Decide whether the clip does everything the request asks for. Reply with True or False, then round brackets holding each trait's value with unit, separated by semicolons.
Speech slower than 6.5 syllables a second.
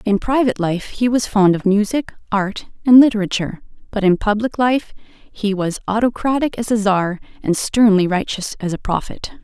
True (5.0 syllables/s)